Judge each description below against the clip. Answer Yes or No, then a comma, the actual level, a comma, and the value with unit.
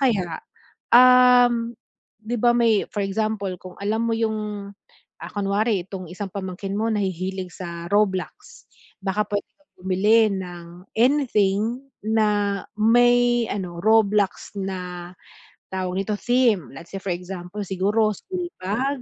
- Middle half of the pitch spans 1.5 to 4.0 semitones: Yes, average, 3.3 semitones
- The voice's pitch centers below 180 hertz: No, high, 205 Hz